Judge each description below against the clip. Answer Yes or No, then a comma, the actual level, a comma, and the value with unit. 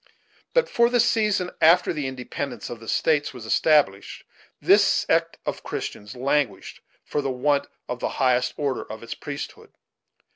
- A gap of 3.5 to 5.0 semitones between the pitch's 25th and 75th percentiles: Yes, average, 4.2 semitones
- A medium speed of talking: Yes, average, 155 wpm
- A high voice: No, medium, 140 Hz